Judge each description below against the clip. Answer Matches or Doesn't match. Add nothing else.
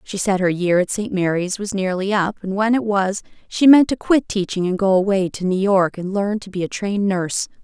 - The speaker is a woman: Matches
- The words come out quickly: Matches